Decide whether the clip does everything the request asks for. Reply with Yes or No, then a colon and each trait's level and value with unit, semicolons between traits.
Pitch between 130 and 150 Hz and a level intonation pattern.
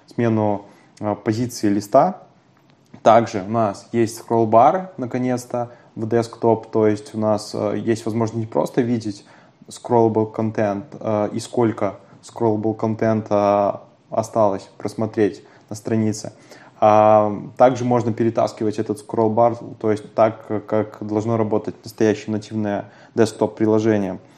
No: low, 110 Hz; narrow, 1.7 semitones